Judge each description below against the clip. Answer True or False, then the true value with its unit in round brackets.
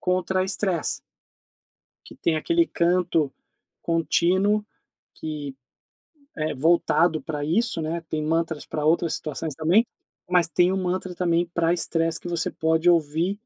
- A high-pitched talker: False (170 Hz)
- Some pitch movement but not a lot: False (2.3 semitones)